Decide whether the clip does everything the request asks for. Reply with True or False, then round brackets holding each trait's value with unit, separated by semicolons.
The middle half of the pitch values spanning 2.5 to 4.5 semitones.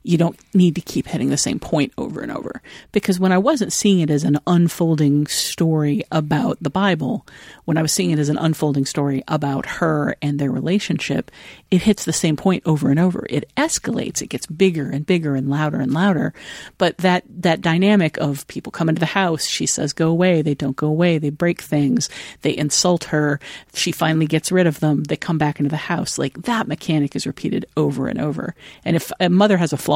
True (3.3 semitones)